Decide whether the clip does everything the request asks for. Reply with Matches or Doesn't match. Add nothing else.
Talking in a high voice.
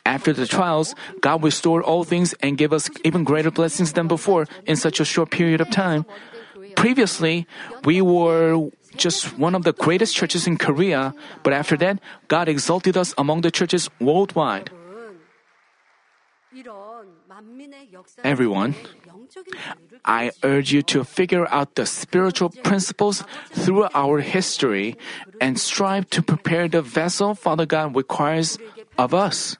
Doesn't match